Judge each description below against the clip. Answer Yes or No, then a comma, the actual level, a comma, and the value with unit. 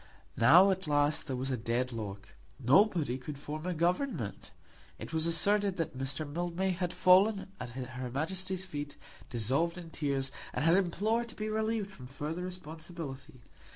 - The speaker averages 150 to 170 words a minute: Yes, average, 160 wpm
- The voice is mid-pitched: Yes, medium, 160 Hz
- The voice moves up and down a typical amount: No, wide, 5.7 semitones